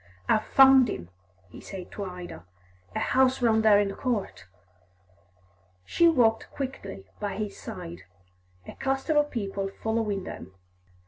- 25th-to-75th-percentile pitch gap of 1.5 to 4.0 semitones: No, average, 5.2 semitones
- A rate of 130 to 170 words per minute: Yes, average, 140 wpm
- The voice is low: No, high, 215 Hz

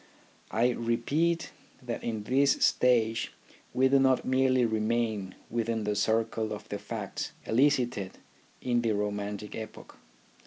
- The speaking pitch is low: Yes, low, 115 Hz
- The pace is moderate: No, slow, 125 wpm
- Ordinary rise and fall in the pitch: Yes, average, 3.0 semitones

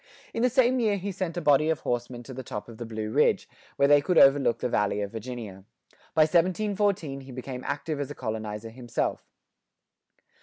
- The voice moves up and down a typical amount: No, wide, 6.8 semitones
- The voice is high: No, low, 135 Hz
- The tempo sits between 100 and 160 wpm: No, average, 195 wpm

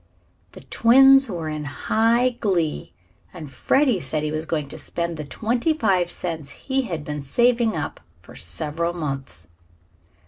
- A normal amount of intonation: No, wide, 7.5 semitones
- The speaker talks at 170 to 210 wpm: No, average, 150 wpm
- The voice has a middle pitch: Yes, medium, 170 Hz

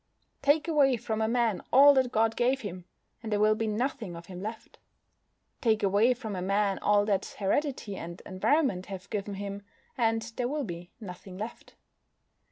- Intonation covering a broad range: No, average, 3.9 semitones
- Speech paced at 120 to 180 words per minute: Yes, average, 175 wpm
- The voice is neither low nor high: No, high, 215 Hz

